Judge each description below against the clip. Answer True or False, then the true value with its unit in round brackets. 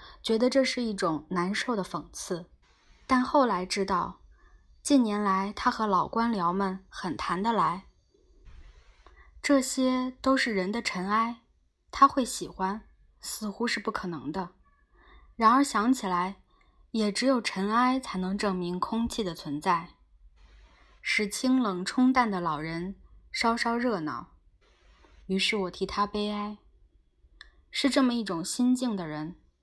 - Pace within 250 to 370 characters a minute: False (190 characters per minute)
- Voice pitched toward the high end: True (210 Hz)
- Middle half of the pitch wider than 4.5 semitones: True (5.1 semitones)